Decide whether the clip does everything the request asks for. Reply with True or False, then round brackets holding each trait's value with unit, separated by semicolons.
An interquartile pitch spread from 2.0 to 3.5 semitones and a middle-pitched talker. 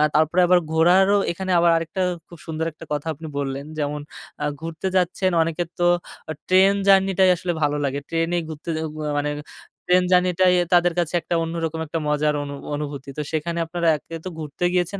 True (2.8 semitones; 165 Hz)